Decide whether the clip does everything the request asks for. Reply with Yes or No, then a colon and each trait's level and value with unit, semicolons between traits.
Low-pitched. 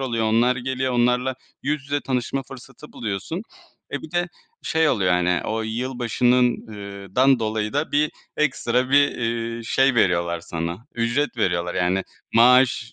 Yes: low, 120 Hz